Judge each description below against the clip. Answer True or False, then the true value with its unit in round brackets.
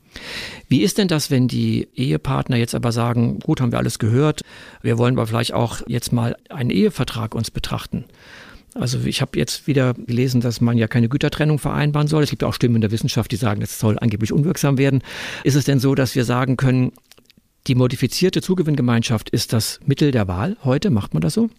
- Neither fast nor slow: False (210 wpm)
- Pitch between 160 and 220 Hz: False (125 Hz)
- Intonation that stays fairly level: False (3.8 semitones)